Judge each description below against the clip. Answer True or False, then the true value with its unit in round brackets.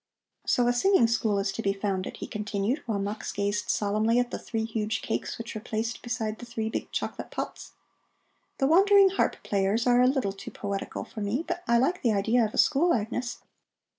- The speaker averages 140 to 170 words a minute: False (205 wpm)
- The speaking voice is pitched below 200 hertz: False (225 Hz)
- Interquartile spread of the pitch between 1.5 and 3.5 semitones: True (3.1 semitones)